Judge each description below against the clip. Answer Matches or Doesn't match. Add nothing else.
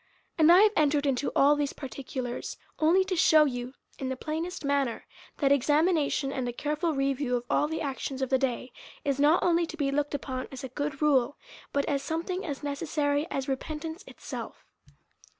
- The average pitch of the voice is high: Matches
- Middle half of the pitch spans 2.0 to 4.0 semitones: Matches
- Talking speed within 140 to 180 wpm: Doesn't match